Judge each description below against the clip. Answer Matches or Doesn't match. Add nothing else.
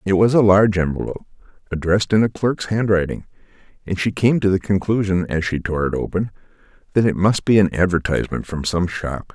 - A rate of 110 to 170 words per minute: Doesn't match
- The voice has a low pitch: Matches